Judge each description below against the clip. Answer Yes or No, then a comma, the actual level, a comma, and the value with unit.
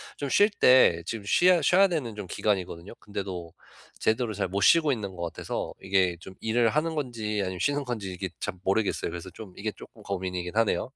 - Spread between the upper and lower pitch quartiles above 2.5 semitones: Yes, average, 5.2 semitones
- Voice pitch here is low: Yes, low, 105 Hz